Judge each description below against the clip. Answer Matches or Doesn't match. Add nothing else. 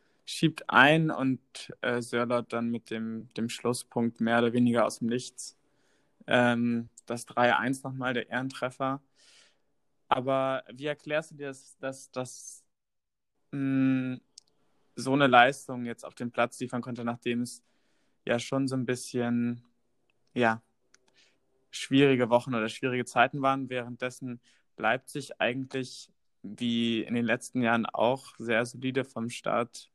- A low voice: Matches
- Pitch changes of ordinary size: Doesn't match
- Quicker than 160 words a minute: Doesn't match